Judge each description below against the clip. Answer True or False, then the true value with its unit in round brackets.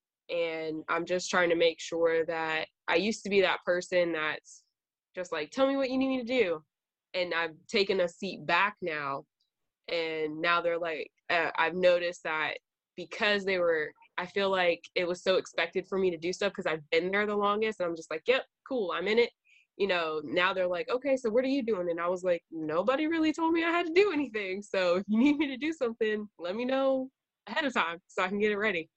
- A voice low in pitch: False (190 Hz)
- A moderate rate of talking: False (235 wpm)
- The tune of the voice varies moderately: False (7.0 semitones)